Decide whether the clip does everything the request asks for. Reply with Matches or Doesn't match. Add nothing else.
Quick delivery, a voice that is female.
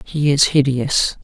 Doesn't match